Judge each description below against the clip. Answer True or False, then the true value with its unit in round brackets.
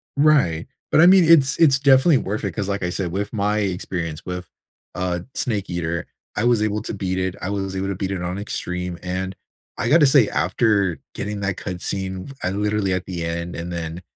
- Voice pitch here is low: True (95 Hz)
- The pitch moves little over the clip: False (3.0 semitones)